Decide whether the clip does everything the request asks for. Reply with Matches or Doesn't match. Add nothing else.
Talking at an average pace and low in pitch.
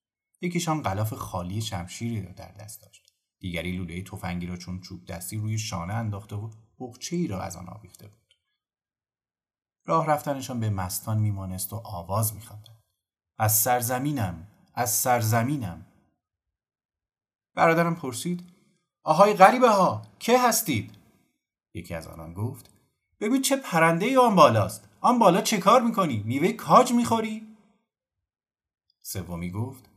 Matches